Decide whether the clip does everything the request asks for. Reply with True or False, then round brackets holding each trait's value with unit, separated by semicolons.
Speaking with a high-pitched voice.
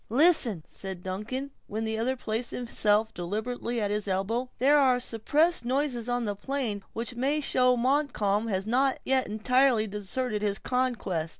True (235 Hz)